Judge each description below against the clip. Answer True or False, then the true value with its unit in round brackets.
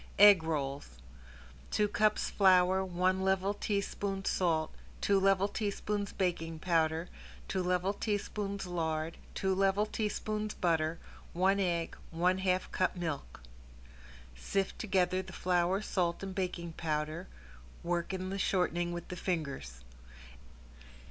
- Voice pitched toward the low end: False (185 Hz)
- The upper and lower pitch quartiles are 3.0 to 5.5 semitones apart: False (2.5 semitones)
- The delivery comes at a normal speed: False (120 wpm)